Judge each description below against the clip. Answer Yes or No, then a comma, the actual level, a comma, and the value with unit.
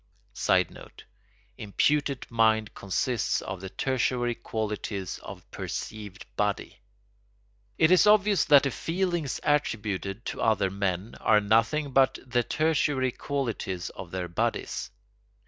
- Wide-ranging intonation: Yes, wide, 5.9 semitones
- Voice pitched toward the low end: Yes, low, 115 Hz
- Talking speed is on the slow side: Yes, slow, 115 wpm